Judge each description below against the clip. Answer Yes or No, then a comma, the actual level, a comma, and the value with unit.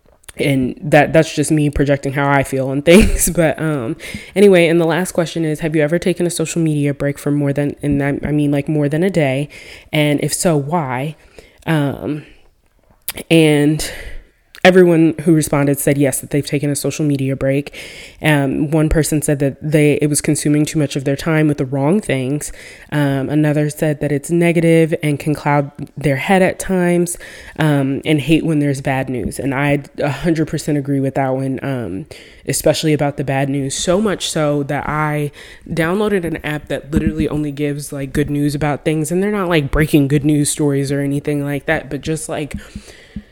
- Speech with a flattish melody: Yes, narrow, 2.0 semitones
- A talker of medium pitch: Yes, medium, 150 Hz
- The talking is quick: No, average, 195 wpm